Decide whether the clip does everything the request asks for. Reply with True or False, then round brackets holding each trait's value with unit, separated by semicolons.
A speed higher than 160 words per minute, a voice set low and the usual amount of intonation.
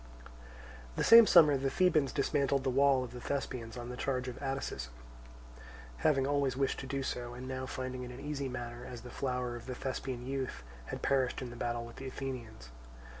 False (200 wpm; 130 Hz; 1.9 semitones)